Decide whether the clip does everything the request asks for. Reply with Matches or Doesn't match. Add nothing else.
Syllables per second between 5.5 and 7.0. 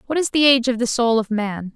Matches